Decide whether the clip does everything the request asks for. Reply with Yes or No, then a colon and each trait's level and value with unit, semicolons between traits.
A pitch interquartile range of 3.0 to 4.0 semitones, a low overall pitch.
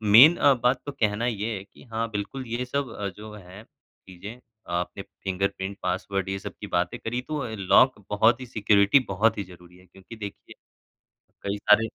Yes: average, 3.6 semitones; low, 105 Hz